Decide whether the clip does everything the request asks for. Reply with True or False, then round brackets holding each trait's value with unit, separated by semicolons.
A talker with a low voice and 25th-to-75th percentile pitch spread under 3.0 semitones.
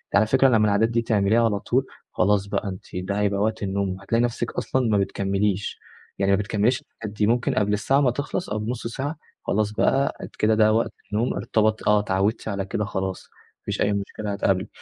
True (105 Hz; 2.4 semitones)